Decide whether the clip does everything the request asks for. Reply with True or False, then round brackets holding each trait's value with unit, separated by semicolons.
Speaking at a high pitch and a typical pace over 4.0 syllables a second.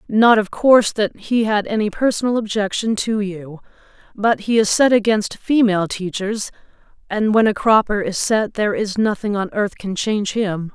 True (210 Hz; 4.9 syllables/s)